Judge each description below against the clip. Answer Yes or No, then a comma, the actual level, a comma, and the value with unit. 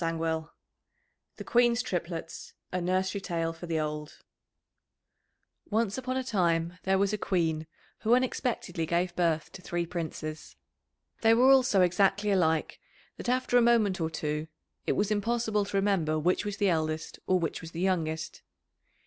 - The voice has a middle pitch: Yes, medium, 180 Hz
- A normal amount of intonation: Yes, average, 4.3 semitones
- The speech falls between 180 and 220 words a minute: No, average, 160 wpm